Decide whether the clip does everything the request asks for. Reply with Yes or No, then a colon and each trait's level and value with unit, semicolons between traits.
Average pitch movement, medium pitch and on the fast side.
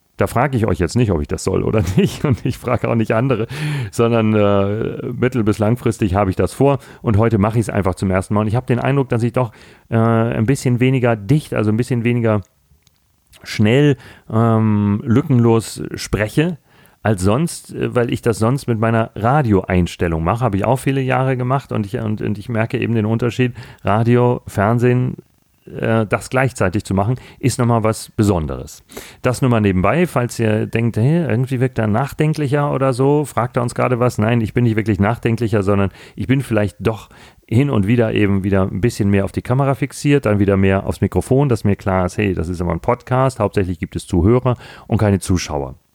No: average, 3.7 semitones; low, 115 Hz; fast, 205 wpm